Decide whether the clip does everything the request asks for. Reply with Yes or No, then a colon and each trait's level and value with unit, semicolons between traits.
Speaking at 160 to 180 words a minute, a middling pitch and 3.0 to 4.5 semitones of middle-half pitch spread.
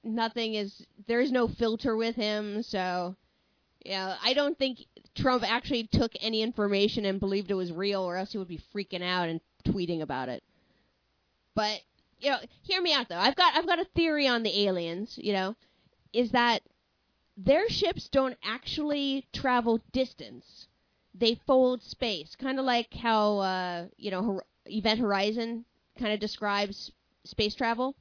No: average, 165 wpm; high, 220 Hz; average, 4.0 semitones